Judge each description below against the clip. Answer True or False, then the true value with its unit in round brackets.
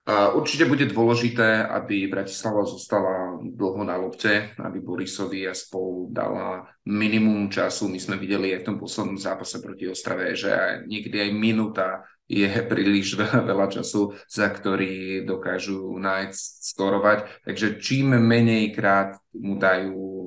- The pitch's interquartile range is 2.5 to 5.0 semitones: False (2.1 semitones)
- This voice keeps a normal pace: True (135 wpm)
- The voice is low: True (100 Hz)